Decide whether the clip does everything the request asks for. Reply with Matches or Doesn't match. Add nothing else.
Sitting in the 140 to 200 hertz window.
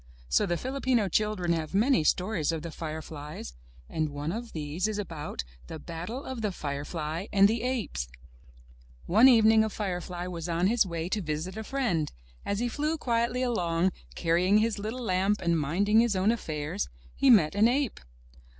Matches